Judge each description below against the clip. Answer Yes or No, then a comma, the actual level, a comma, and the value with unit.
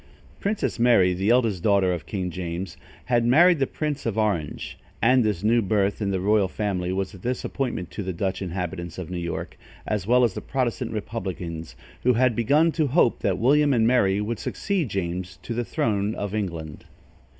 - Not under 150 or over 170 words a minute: No, average, 190 wpm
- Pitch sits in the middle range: No, low, 105 Hz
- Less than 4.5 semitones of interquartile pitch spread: No, average, 4.8 semitones